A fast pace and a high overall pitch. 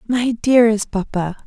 No: slow, 125 wpm; high, 220 Hz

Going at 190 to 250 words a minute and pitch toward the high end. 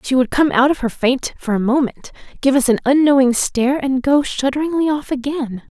Yes: fast, 205 wpm; very high, 265 Hz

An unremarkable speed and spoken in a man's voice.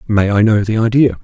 No: fast, 245 wpm; male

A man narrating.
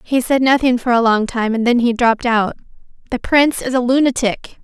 No: female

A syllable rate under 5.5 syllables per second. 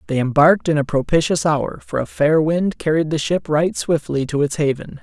Yes: 5.2 syllables/s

